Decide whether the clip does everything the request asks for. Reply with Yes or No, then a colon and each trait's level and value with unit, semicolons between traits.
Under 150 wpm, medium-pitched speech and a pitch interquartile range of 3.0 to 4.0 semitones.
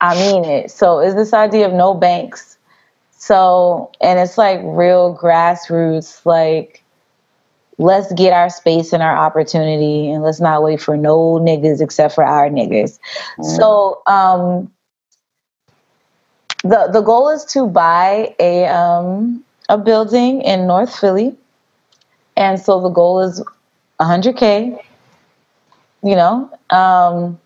Yes: slow, 135 wpm; medium, 180 Hz; average, 3.7 semitones